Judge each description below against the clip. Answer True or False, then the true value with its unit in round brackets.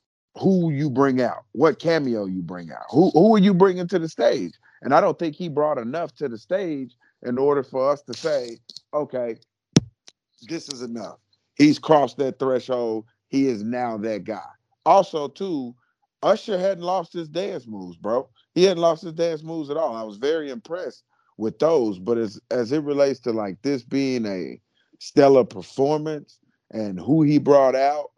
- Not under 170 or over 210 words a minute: True (185 wpm)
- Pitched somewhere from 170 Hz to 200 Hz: False (140 Hz)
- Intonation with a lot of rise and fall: True (5.7 semitones)